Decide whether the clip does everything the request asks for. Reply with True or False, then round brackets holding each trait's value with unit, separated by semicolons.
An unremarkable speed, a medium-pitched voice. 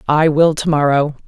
True (190 wpm; 150 Hz)